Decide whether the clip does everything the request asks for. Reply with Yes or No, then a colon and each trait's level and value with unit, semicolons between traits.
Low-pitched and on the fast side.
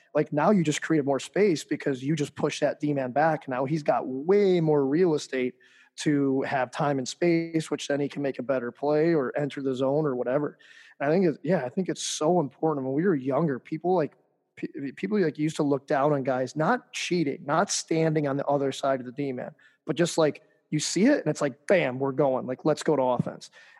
No: medium, 150 Hz; fast, 230 wpm